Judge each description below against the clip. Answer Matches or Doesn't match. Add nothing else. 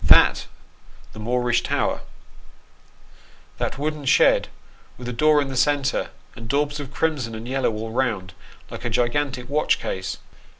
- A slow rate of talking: Doesn't match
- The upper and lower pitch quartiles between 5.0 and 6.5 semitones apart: Doesn't match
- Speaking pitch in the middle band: Doesn't match